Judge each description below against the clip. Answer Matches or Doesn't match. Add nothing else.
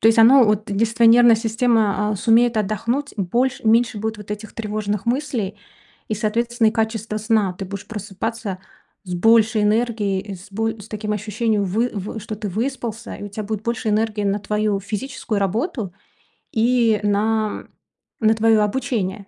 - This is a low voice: Doesn't match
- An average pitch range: Doesn't match